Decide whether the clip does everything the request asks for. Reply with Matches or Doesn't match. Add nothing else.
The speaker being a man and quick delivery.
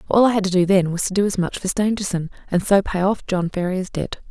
Doesn't match